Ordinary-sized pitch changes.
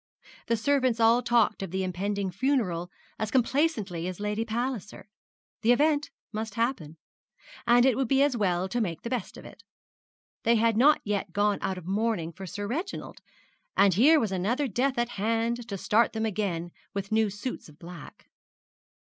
Yes: average, 4.0 semitones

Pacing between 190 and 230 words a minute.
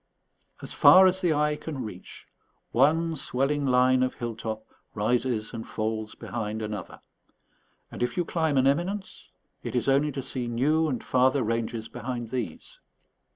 No: average, 155 wpm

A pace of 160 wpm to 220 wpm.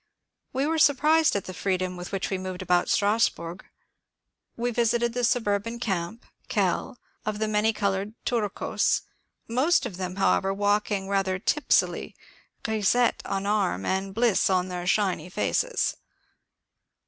No: slow, 135 wpm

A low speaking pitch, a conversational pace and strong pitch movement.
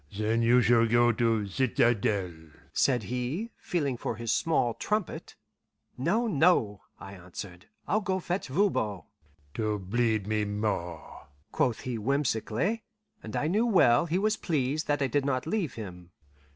Yes: low, 120 Hz; average, 150 wpm; wide, 6.8 semitones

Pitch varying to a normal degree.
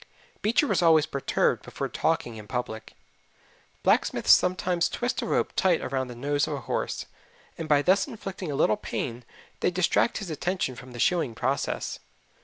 No: wide, 6.1 semitones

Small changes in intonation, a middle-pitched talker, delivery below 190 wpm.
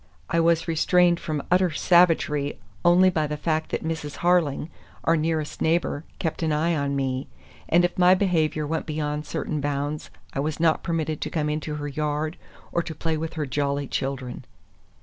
Yes: narrow, 2.3 semitones; medium, 155 Hz; average, 180 wpm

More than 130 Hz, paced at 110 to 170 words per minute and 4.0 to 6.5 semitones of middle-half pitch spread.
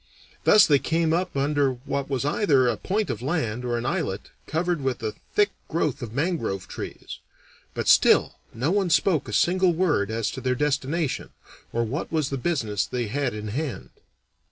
No: medium, 140 Hz; average, 180 wpm; wide, 5.5 semitones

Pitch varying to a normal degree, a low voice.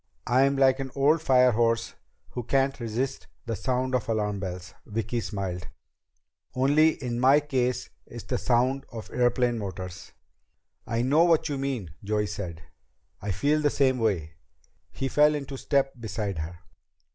Yes: average, 4.5 semitones; low, 125 Hz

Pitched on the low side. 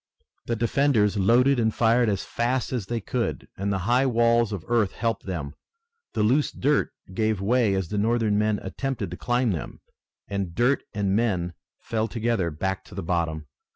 Yes: low, 110 Hz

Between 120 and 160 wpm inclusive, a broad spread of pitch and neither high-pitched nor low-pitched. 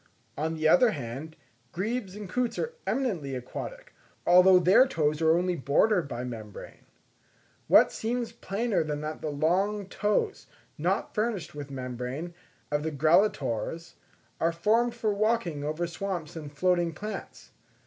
Yes: average, 140 wpm; wide, 6.0 semitones; medium, 170 Hz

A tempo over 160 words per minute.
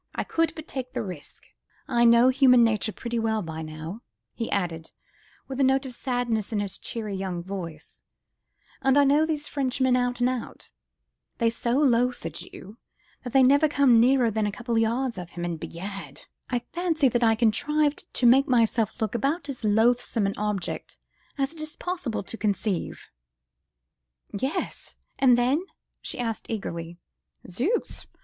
Yes: average, 170 wpm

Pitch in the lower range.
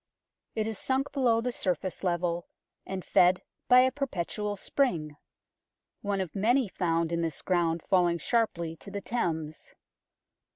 No: medium, 185 Hz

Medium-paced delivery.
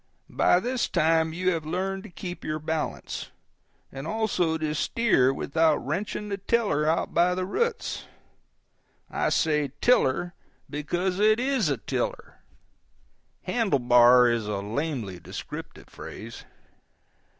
No: slow, 130 wpm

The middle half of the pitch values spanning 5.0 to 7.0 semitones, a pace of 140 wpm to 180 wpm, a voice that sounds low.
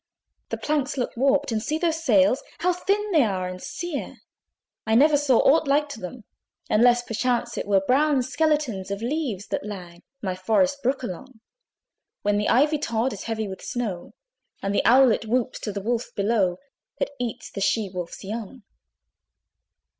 No: wide, 5.6 semitones; average, 170 wpm; high, 240 Hz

